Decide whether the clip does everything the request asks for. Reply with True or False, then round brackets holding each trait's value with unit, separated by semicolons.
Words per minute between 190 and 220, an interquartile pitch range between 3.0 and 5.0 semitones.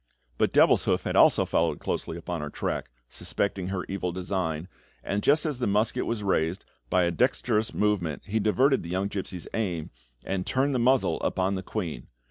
False (180 wpm; 3.7 semitones)